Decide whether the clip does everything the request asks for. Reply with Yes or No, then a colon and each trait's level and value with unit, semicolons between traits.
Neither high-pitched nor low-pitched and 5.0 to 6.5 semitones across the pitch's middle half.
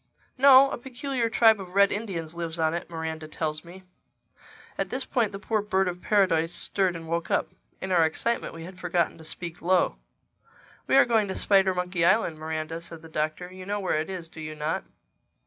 No: medium, 180 Hz; average, 3.8 semitones